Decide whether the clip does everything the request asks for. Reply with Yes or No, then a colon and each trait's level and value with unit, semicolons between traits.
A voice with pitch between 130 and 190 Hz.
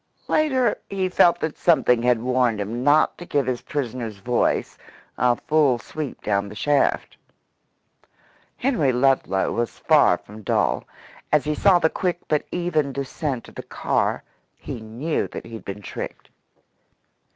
Yes: low, 135 Hz